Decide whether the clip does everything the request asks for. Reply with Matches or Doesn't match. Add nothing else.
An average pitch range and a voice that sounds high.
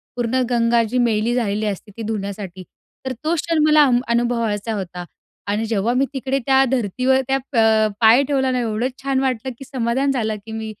Matches